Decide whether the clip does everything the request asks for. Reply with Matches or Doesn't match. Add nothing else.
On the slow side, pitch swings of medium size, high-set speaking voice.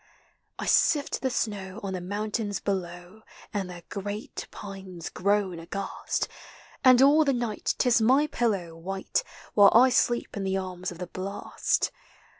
Doesn't match